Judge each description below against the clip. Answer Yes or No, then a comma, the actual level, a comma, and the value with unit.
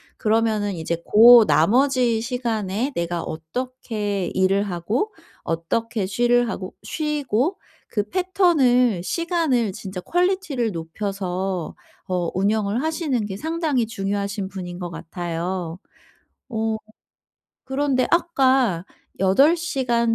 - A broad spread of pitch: Yes, wide, 5.7 semitones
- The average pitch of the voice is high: Yes, high, 220 Hz